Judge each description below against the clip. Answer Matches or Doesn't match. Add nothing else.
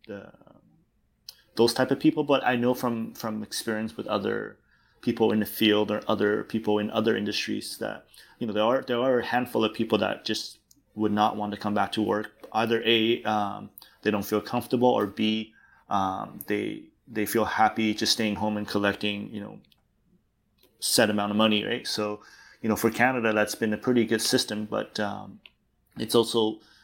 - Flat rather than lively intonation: Matches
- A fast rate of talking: Doesn't match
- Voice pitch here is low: Matches